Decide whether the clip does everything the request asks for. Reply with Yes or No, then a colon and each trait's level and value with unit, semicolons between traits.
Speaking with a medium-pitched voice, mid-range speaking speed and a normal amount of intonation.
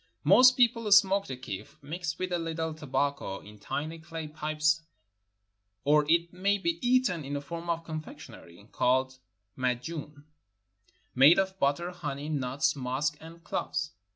Yes: medium, 155 Hz; average, 150 wpm; average, 3.5 semitones